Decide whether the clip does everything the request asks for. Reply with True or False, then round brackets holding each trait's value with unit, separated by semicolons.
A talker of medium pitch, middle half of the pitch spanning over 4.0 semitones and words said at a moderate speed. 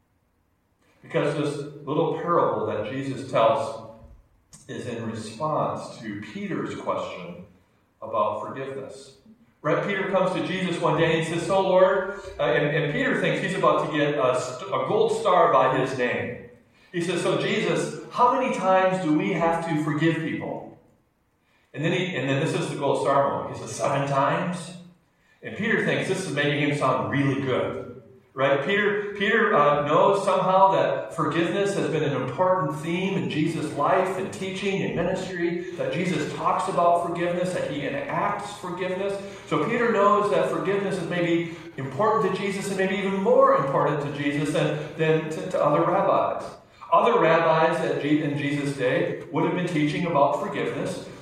True (165 Hz; 4.7 semitones; 170 wpm)